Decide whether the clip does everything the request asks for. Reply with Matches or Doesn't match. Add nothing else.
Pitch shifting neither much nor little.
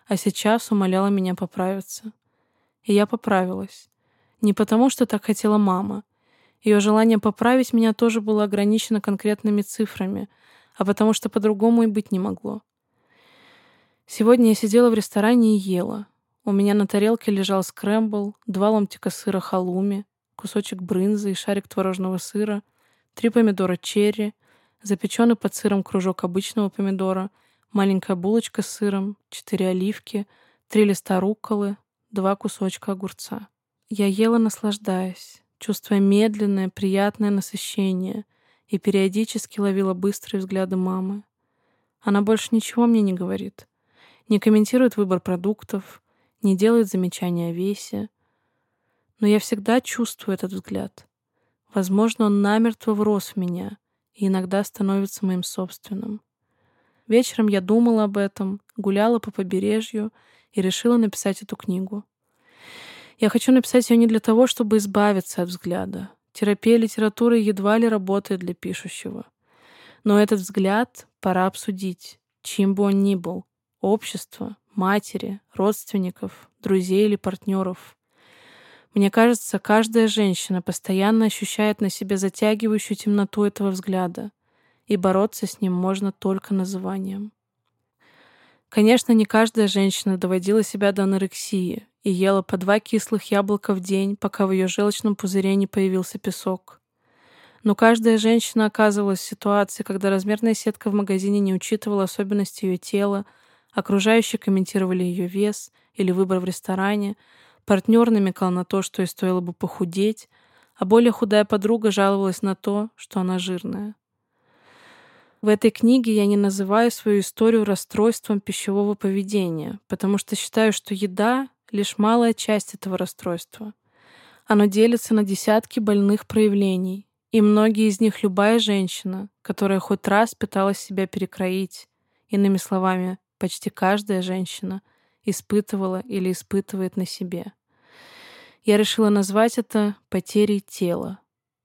Doesn't match